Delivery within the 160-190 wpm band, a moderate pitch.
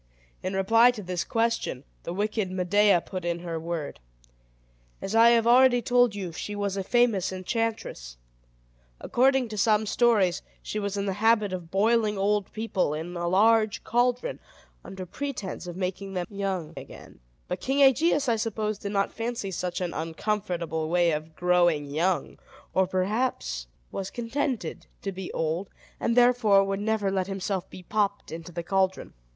No: average, 165 wpm; high, 195 Hz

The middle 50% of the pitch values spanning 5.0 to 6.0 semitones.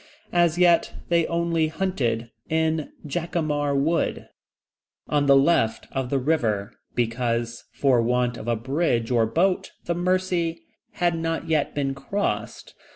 Yes: wide, 5.5 semitones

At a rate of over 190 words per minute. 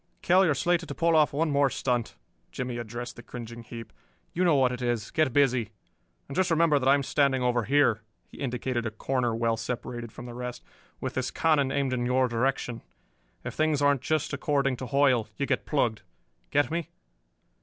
Yes: average, 200 wpm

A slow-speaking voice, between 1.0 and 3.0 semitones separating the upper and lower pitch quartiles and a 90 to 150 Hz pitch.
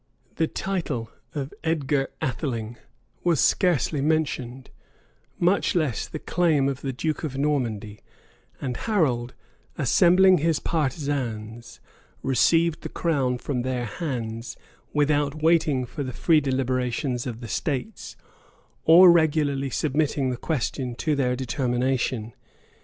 No: slow, 120 wpm; average, 4.1 semitones; medium, 140 Hz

